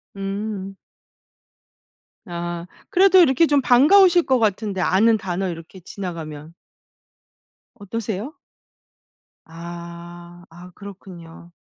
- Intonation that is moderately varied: Yes, average, 4.7 semitones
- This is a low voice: No, high, 190 Hz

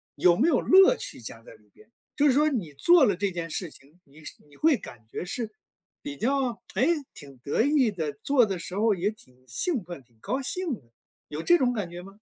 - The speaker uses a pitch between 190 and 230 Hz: Yes, high, 200 Hz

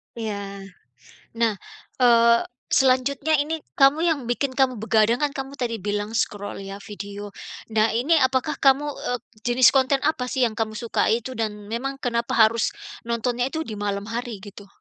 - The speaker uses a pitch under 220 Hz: No, high, 240 Hz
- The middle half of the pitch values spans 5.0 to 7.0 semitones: No, average, 3.8 semitones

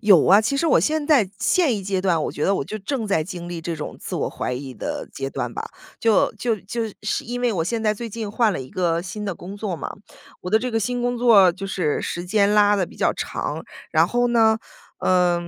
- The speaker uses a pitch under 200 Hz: No, high, 205 Hz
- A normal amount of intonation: Yes, average, 4.6 semitones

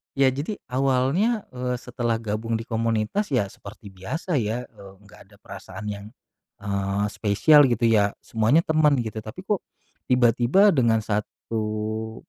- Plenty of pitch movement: No, average, 3.9 semitones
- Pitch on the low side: Yes, low, 115 Hz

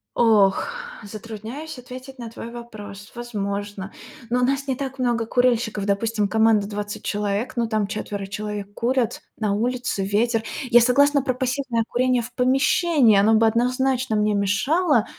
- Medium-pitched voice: No, high, 230 Hz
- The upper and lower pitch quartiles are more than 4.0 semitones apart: No, average, 3.4 semitones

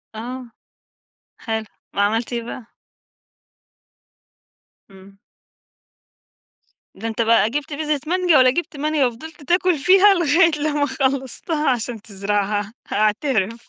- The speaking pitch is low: No, very high, 255 Hz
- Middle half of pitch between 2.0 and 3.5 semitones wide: No, wide, 5.5 semitones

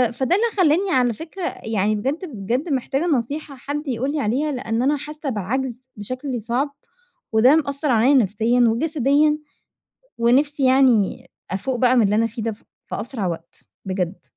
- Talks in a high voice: Yes, very high, 255 Hz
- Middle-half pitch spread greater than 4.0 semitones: Yes, average, 4.4 semitones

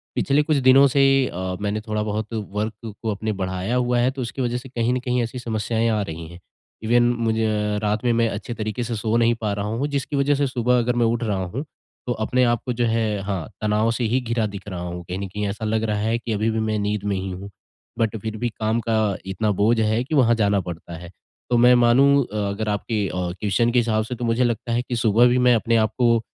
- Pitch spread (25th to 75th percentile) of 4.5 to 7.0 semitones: No, average, 2.7 semitones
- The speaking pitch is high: No, low, 115 Hz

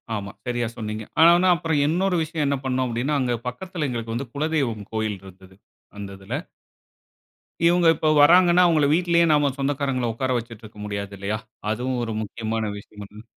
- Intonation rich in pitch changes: Yes, wide, 6.2 semitones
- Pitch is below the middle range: Yes, low, 125 Hz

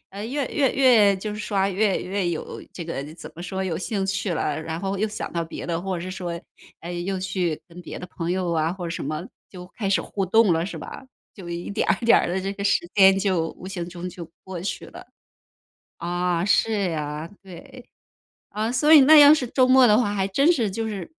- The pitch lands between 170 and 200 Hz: Yes, high, 190 Hz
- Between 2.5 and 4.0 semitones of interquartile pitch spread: Yes, average, 3.4 semitones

